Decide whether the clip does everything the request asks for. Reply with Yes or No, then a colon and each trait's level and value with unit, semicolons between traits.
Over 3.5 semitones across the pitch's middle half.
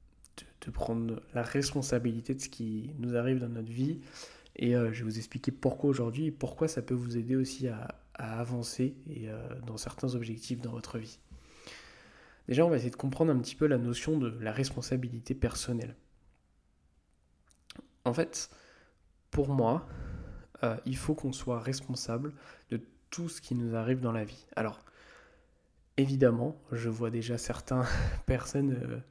No: narrow, 2.6 semitones